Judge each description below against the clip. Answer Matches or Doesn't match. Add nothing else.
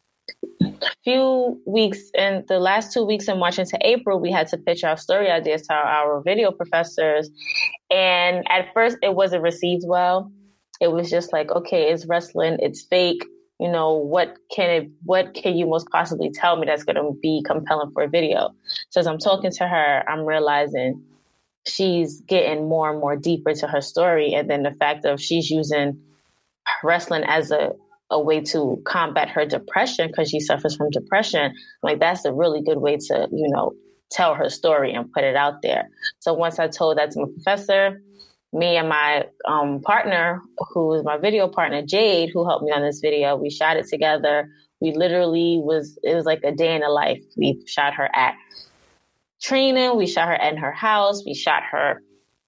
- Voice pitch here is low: Doesn't match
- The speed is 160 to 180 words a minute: Doesn't match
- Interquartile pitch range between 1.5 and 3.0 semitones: Doesn't match